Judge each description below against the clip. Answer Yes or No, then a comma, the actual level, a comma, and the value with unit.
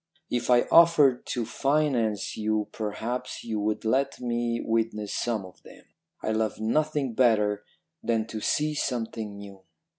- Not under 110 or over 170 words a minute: Yes, average, 145 wpm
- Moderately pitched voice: No, low, 115 Hz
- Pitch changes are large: No, average, 2.8 semitones